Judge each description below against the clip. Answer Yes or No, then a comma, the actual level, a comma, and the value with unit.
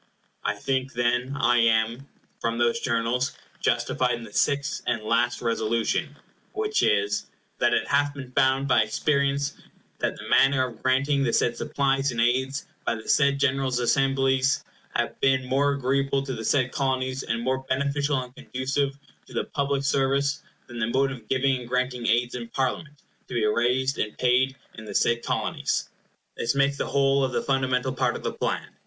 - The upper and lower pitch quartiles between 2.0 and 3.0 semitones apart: Yes, narrow, 2.5 semitones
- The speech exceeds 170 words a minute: Yes, average, 180 wpm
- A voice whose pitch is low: Yes, low, 130 Hz